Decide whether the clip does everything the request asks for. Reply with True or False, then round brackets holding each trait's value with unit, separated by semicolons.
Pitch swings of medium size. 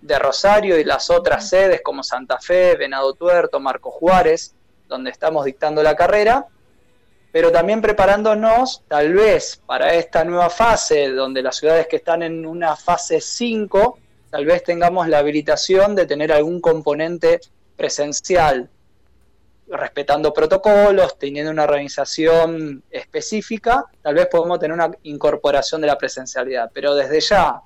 False (6.1 semitones)